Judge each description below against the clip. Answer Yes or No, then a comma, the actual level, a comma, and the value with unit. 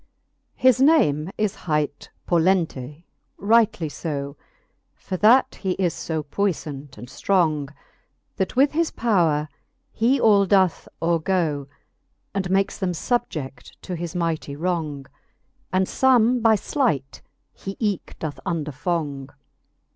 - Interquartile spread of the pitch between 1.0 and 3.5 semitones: No, average, 5.2 semitones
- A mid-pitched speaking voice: Yes, medium, 175 Hz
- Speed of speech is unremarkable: No, slow, 120 wpm